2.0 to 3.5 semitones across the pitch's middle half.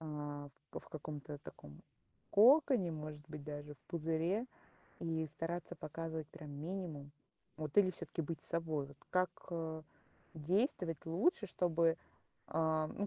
Yes: narrow, 2.6 semitones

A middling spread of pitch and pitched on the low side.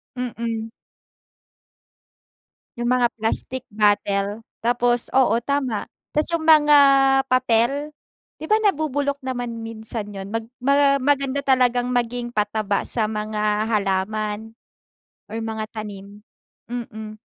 No: average, 3.4 semitones; high, 235 Hz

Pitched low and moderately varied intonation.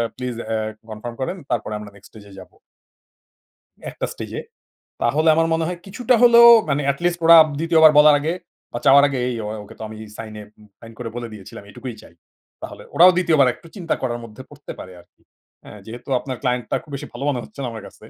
No: low, 130 Hz; wide, 6.1 semitones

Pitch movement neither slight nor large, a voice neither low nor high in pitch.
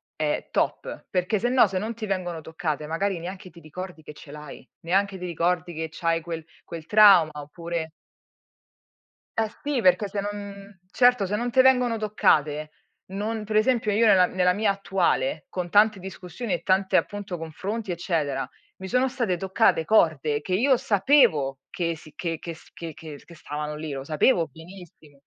Yes: average, 4.3 semitones; medium, 180 Hz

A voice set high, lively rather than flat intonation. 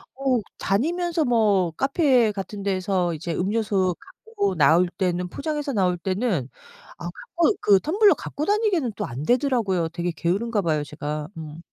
Yes: high, 200 Hz; wide, 7.8 semitones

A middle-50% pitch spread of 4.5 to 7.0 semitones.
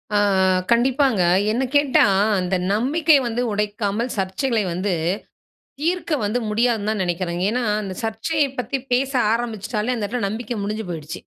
No: average, 3.7 semitones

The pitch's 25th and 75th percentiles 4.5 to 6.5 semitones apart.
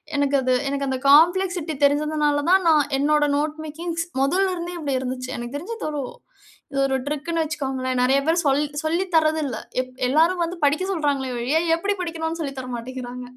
No: average, 3.6 semitones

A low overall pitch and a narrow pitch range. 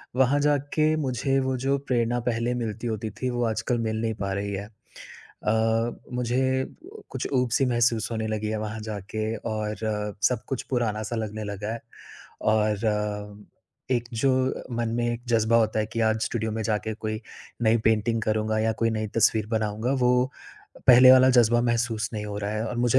Yes: low, 115 Hz; narrow, 2.2 semitones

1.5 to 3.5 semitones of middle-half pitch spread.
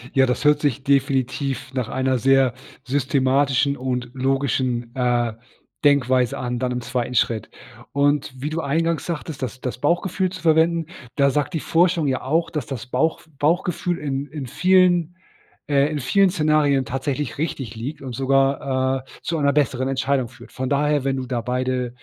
Yes: average, 2.8 semitones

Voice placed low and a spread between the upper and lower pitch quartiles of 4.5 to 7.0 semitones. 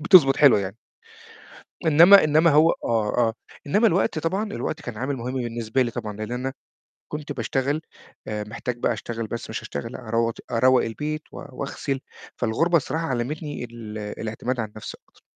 Yes: low, 125 Hz; average, 4.9 semitones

